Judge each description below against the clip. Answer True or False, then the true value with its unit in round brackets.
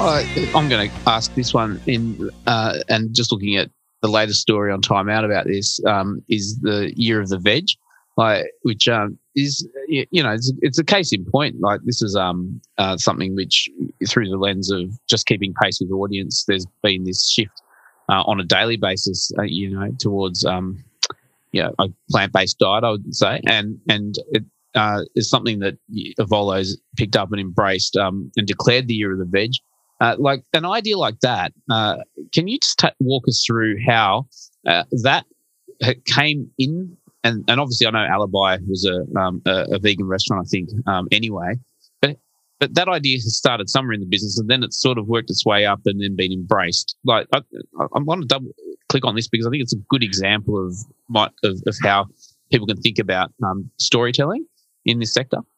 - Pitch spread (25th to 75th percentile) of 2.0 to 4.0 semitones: False (4.6 semitones)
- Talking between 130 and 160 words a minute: False (205 wpm)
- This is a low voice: True (110 Hz)